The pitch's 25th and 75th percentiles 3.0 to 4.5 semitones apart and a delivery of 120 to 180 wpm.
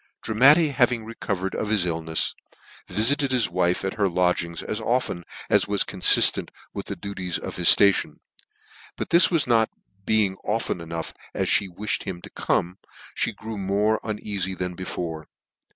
Yes: average, 3.7 semitones; average, 165 wpm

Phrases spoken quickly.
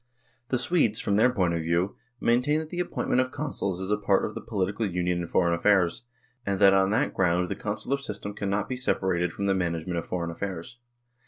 Yes: fast, 215 wpm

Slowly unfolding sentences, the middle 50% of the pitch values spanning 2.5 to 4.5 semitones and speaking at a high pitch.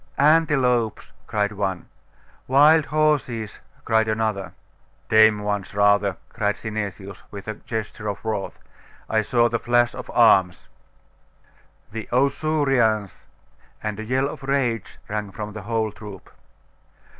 No: slow, 120 wpm; average, 3.2 semitones; low, 110 Hz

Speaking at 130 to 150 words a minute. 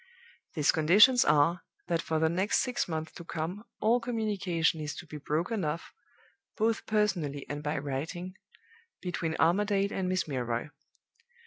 Yes: average, 145 wpm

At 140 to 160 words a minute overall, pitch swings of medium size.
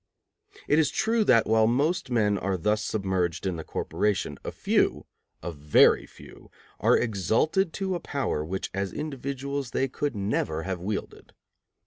No: average, 155 wpm; wide, 6.6 semitones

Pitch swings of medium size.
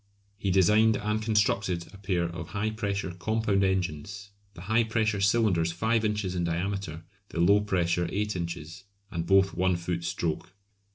Yes: average, 3.4 semitones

